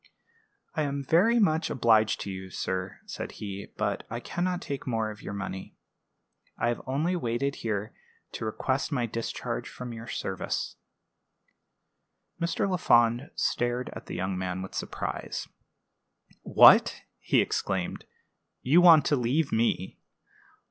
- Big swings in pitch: Yes, wide, 5.7 semitones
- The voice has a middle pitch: No, low, 120 Hz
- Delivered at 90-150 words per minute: Yes, average, 140 wpm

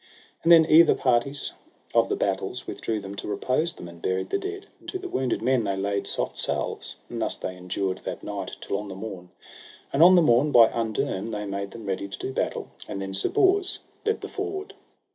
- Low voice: Yes, low, 115 Hz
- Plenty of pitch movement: Yes, wide, 9.0 semitones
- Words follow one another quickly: Yes, fast, 220 wpm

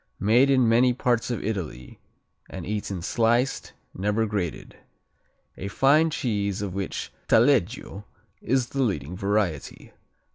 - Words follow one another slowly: Yes, slow, 120 wpm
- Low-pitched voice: Yes, low, 110 Hz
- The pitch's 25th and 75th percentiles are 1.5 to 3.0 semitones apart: No, average, 4.0 semitones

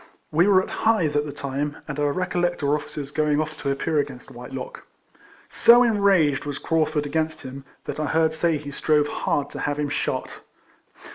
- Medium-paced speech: Yes, average, 190 wpm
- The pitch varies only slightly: Yes, narrow, 2.1 semitones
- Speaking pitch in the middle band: Yes, medium, 150 Hz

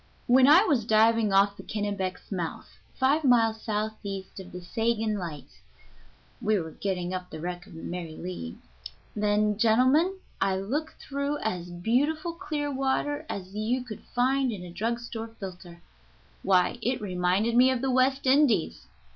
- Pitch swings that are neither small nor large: No, wide, 5.7 semitones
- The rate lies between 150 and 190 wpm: Yes, average, 160 wpm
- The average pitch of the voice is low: No, high, 220 Hz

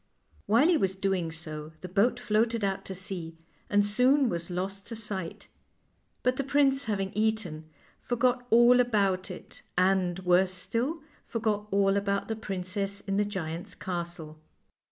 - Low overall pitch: No, high, 200 Hz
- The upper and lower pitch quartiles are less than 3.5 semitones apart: No, average, 4.0 semitones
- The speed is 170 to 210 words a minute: No, average, 155 wpm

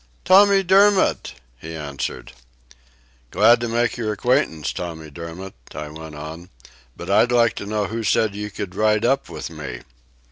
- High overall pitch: No, low, 105 Hz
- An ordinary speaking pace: Yes, average, 155 wpm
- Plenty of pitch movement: Yes, wide, 6.9 semitones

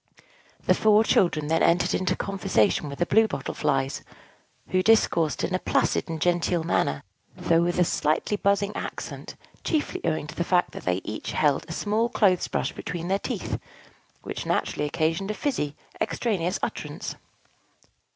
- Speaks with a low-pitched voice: No, medium, 175 Hz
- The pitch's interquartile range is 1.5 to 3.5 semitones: No, average, 4.2 semitones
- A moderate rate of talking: Yes, average, 160 wpm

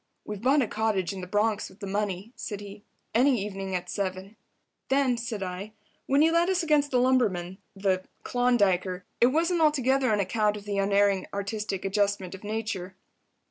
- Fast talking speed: No, average, 165 wpm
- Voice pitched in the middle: No, high, 205 Hz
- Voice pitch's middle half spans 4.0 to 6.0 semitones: Yes, average, 4.3 semitones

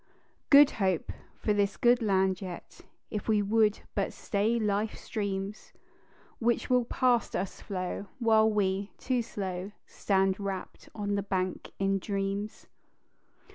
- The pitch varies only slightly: Yes, narrow, 2.3 semitones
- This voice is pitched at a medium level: No, high, 205 Hz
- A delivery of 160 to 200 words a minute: No, slow, 135 wpm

